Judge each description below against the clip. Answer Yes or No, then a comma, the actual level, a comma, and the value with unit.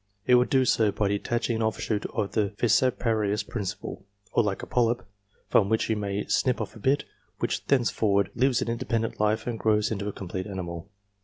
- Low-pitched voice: Yes, low, 110 Hz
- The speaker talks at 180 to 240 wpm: Yes, average, 190 wpm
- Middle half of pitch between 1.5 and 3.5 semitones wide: Yes, average, 2.7 semitones